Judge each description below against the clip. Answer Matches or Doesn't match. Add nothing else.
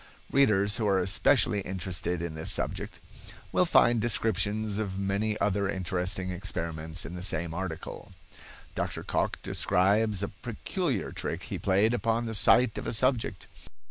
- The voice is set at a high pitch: Doesn't match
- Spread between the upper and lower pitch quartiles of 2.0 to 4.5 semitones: Matches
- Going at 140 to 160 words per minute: Matches